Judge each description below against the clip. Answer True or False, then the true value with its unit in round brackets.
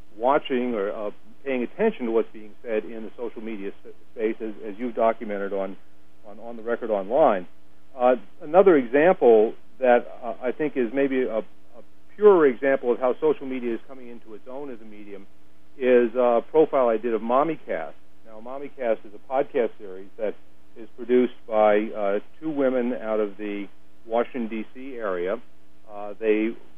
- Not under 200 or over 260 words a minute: False (180 wpm)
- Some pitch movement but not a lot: True (3.6 semitones)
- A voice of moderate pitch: False (115 Hz)